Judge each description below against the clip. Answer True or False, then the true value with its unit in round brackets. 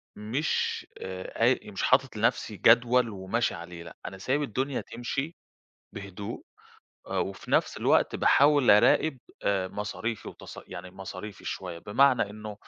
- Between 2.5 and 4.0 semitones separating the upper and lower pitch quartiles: False (4.7 semitones)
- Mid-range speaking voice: False (105 Hz)